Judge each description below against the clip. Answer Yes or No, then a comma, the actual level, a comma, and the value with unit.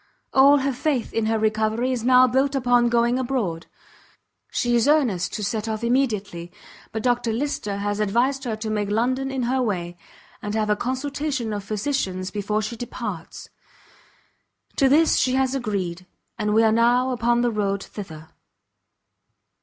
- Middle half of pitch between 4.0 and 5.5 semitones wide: No, average, 3.6 semitones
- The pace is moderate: Yes, average, 160 wpm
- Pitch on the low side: No, high, 230 Hz